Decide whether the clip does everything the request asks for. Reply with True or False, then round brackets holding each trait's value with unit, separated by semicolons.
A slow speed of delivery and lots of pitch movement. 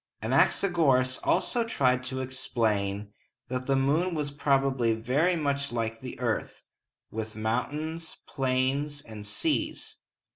False (115 wpm; 4.0 semitones)